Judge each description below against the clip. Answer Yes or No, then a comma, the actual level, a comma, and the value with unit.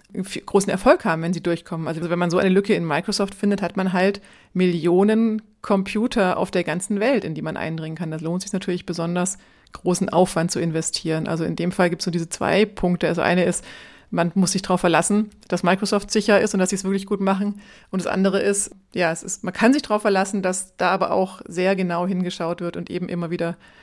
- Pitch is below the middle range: No, medium, 185 Hz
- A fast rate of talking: Yes, fast, 230 wpm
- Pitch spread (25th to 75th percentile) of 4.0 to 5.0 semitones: No, narrow, 2.6 semitones